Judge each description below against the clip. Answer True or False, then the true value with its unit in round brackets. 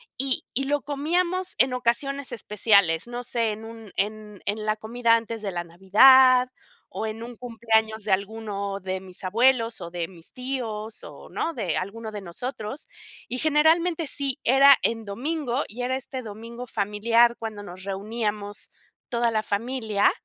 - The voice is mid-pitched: False (230 Hz)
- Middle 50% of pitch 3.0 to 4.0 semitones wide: True (3.7 semitones)